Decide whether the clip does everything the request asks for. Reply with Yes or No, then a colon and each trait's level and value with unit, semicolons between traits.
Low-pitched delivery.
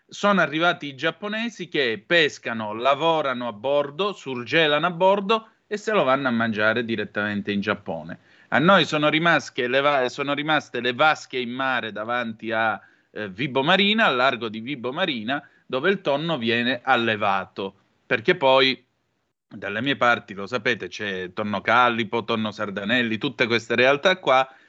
Yes: low, 130 Hz